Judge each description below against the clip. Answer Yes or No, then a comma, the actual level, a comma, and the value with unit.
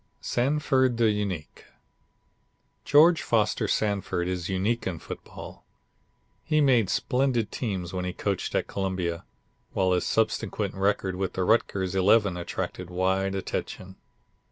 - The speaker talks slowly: Yes, slow, 125 wpm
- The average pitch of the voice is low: Yes, very low, 95 Hz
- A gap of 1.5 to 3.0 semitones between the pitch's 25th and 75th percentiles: No, average, 3.8 semitones